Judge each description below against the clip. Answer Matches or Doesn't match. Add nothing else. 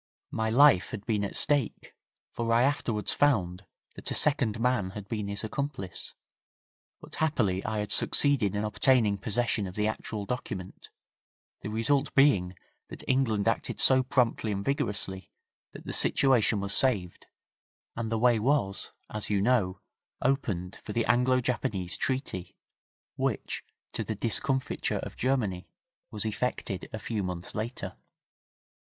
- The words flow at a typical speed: Matches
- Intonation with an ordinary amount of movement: Matches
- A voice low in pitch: Matches